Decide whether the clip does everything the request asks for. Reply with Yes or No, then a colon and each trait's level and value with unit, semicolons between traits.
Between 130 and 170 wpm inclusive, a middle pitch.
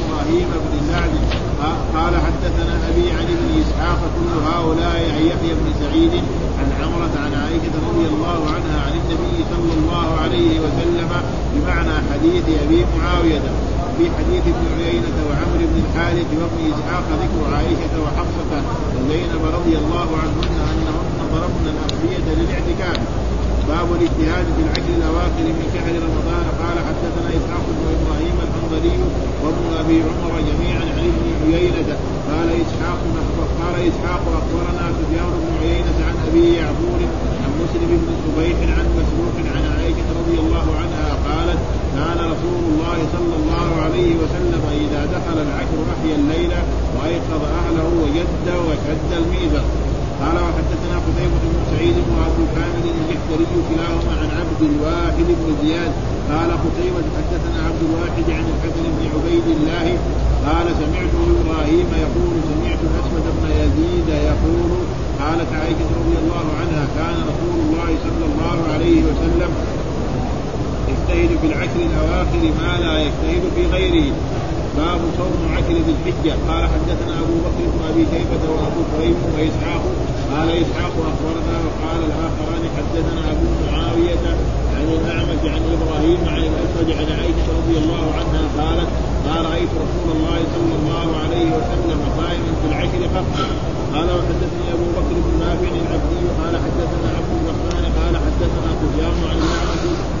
Yes: fast, 135 wpm; medium, 170 Hz